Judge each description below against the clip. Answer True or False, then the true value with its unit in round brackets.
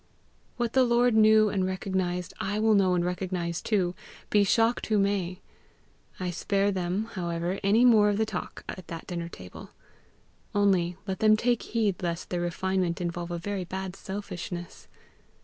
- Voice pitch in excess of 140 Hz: True (190 Hz)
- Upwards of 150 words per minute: True (165 wpm)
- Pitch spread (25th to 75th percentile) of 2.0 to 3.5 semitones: True (3.1 semitones)